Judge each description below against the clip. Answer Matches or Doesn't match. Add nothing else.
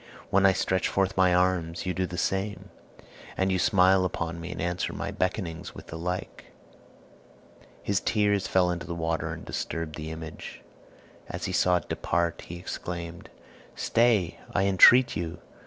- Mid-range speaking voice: Doesn't match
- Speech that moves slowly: Doesn't match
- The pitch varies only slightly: Matches